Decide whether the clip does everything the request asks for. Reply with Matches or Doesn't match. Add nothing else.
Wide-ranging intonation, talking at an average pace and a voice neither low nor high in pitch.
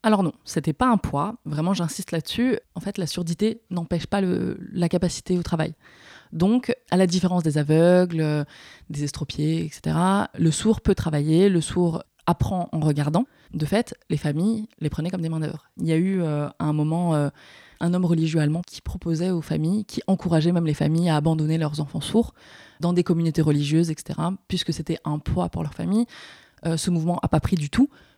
Doesn't match